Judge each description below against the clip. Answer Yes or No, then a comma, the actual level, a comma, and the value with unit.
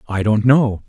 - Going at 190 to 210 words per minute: Yes, fast, 205 wpm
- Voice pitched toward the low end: Yes, low, 115 Hz